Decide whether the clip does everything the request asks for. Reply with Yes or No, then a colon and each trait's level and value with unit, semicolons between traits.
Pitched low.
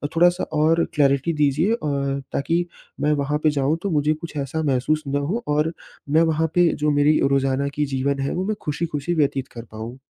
No: medium, 150 Hz